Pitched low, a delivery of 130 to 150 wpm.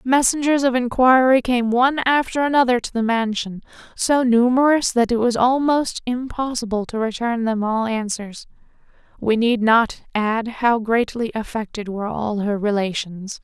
No: high, 235 Hz; average, 145 wpm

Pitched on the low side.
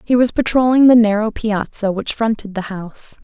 No: high, 220 Hz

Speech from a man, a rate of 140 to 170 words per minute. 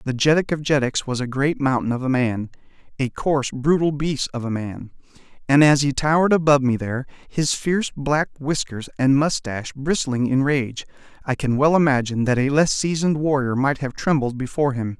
No: male; average, 185 wpm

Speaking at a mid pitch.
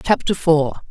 Yes: medium, 165 Hz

